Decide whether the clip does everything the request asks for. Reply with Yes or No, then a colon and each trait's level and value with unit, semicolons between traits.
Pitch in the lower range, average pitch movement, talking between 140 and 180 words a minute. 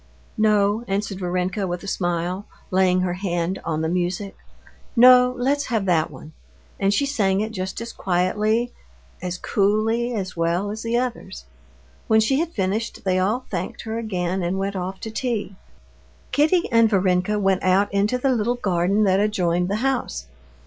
No: high, 200 Hz; average, 3.6 semitones; average, 170 wpm